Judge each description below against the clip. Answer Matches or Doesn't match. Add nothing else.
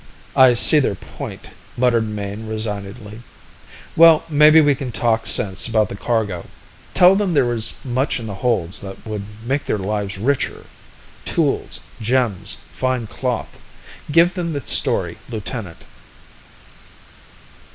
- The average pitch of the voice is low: Matches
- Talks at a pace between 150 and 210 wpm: Doesn't match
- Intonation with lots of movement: Doesn't match